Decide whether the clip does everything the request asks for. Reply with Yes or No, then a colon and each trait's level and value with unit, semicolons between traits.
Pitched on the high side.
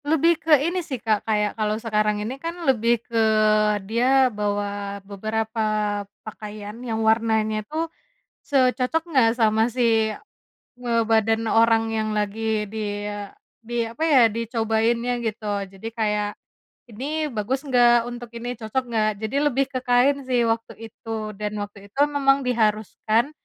Yes: high, 225 Hz